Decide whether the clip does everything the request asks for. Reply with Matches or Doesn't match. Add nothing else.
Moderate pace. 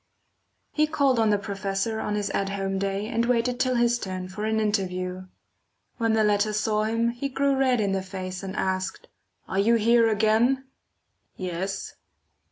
Matches